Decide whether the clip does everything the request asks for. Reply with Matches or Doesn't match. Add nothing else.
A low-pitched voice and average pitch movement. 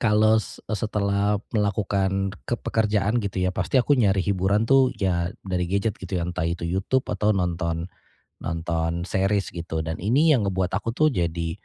Matches